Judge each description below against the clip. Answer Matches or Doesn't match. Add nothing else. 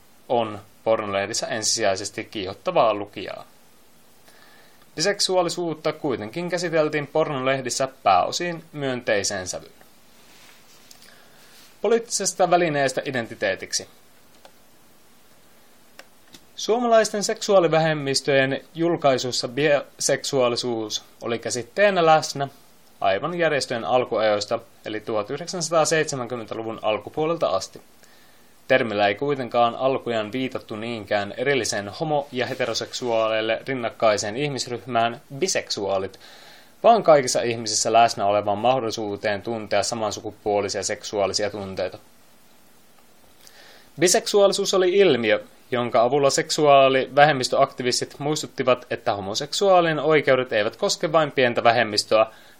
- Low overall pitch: Matches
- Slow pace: Matches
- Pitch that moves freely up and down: Matches